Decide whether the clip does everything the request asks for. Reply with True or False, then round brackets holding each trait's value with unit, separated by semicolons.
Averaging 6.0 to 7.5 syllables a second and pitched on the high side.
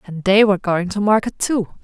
False (5.5 syllables/s; 200 Hz)